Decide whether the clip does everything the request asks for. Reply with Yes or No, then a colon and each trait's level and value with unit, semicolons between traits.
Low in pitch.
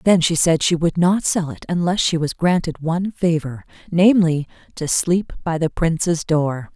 No: medium, 165 Hz